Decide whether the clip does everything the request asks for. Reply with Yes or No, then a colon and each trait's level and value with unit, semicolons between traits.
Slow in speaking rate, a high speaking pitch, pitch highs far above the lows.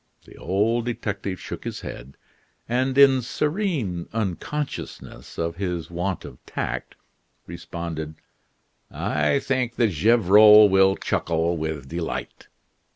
No: slow, 110 wpm; very low, 95 Hz; wide, 6.0 semitones